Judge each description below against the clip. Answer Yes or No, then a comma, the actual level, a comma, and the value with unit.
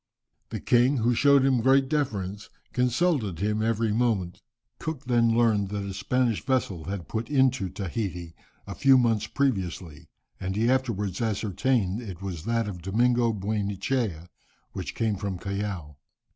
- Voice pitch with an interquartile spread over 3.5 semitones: Yes, average, 4.2 semitones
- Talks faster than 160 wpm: No, average, 150 wpm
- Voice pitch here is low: Yes, low, 110 Hz